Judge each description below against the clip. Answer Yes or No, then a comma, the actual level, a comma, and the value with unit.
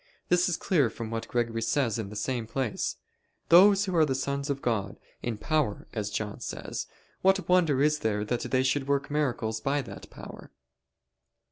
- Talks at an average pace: Yes, average, 175 wpm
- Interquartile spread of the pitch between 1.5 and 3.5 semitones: No, average, 5.2 semitones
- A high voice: No, low, 135 Hz